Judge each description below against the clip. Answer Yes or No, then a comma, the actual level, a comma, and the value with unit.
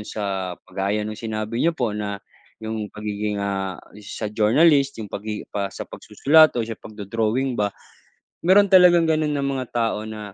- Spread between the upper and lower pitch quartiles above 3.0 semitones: Yes, average, 4.9 semitones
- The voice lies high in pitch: No, low, 110 Hz